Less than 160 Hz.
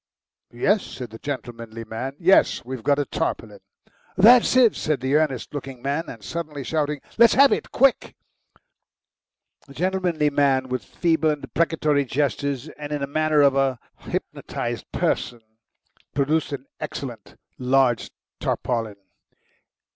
Yes: medium, 140 Hz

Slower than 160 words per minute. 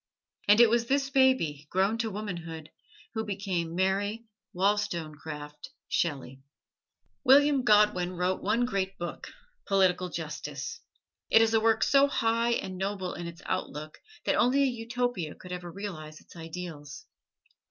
Yes: average, 140 wpm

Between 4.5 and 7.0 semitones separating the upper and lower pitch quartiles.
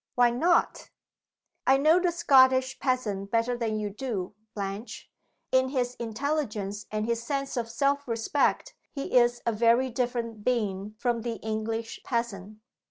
No: average, 3.2 semitones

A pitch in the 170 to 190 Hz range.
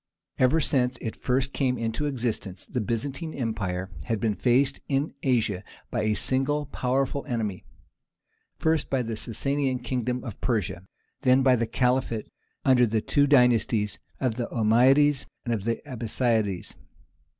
No: low, 125 Hz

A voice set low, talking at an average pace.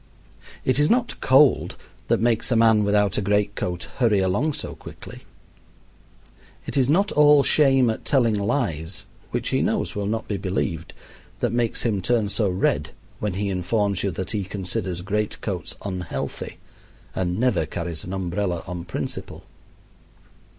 Yes: low, 105 Hz; average, 155 wpm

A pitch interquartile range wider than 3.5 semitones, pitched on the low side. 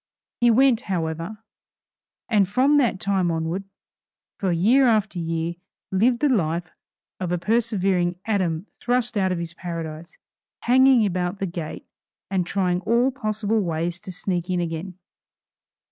No: average, 4.5 semitones; high, 190 Hz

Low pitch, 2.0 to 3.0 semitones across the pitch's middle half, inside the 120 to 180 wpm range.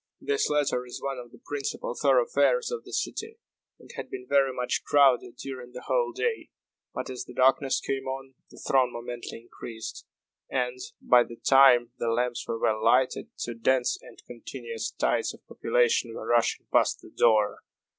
Yes: low, 125 Hz; narrow, 2.4 semitones; average, 175 wpm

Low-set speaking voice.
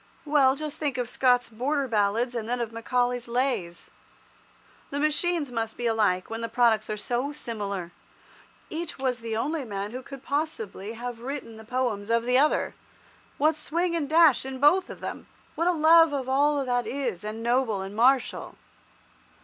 No: very high, 250 Hz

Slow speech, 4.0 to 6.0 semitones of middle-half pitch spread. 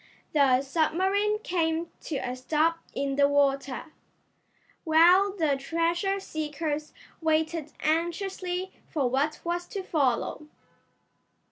No: slow, 105 wpm; average, 3.5 semitones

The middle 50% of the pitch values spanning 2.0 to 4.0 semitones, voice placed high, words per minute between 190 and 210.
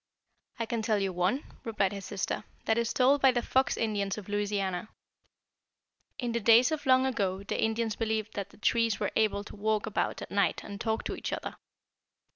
Yes: narrow, 2.5 semitones; high, 220 Hz; average, 200 wpm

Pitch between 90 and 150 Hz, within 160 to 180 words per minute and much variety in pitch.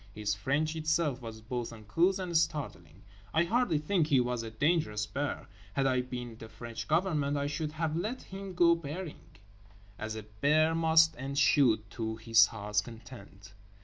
Yes: medium, 140 Hz; average, 170 wpm; wide, 6.2 semitones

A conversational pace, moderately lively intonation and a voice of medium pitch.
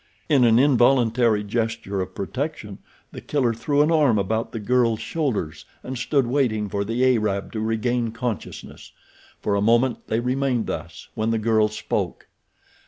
No: average, 160 wpm; average, 3.0 semitones; low, 115 Hz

